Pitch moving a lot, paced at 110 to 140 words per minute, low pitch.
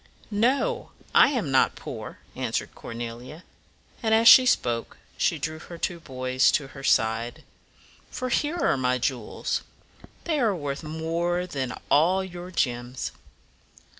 No: wide, 6.7 semitones; slow, 135 wpm; medium, 155 Hz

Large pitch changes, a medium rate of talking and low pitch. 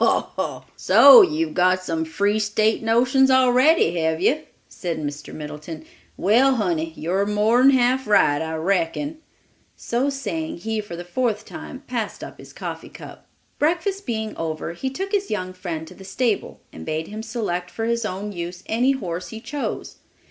No: wide, 6.6 semitones; average, 170 wpm; high, 210 Hz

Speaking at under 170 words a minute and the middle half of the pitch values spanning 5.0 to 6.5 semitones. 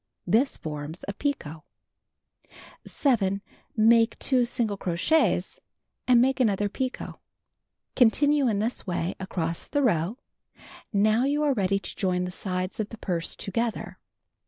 Yes: slow, 135 wpm; average, 5.3 semitones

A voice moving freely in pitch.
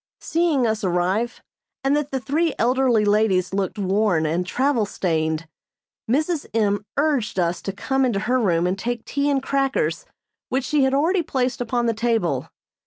Yes: wide, 5.8 semitones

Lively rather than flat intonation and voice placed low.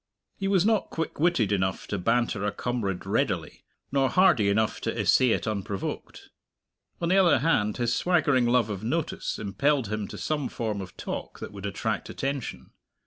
Yes: wide, 6.5 semitones; low, 120 Hz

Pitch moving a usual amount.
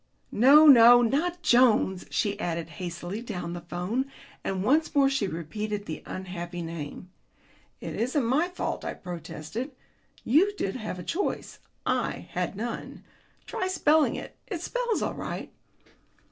No: wide, 8.1 semitones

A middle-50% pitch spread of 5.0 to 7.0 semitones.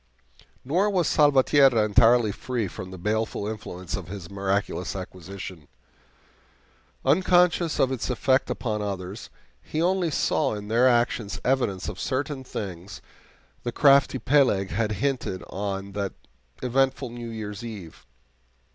Yes: average, 5.3 semitones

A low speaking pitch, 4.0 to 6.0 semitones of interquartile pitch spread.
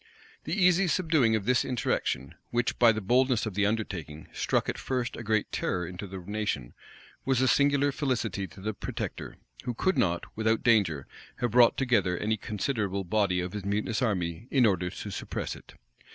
Yes: low, 110 Hz; average, 4.6 semitones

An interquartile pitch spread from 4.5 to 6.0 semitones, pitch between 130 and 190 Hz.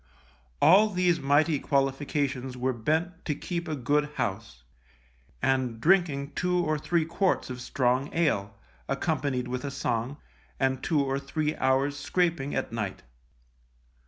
No: average, 3.7 semitones; medium, 140 Hz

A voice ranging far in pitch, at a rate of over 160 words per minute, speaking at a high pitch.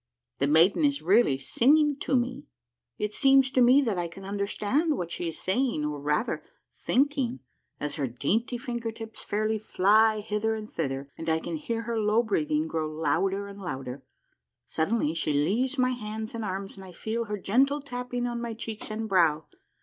Yes: wide, 6.4 semitones; average, 190 wpm; high, 215 Hz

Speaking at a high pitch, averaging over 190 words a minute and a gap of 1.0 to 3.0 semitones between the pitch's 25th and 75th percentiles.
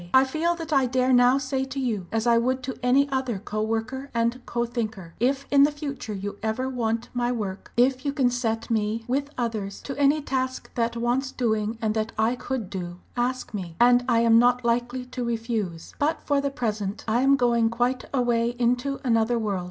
Yes: high, 240 Hz; fast, 205 wpm; average, 2.7 semitones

